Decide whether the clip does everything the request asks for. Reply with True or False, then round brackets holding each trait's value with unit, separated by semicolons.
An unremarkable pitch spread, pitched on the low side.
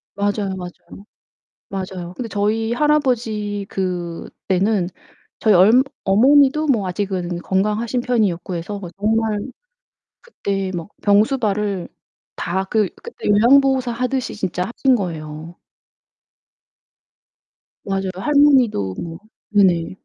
False (4.1 semitones; 205 Hz)